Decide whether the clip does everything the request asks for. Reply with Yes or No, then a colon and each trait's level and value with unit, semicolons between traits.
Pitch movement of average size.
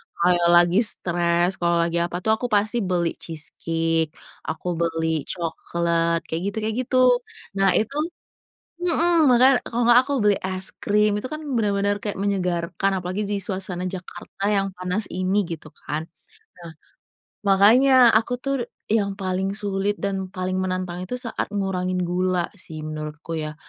Yes: average, 3.2 semitones